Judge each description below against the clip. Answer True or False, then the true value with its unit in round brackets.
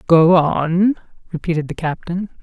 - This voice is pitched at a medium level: True (170 Hz)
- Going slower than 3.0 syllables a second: False (4.4 syllables/s)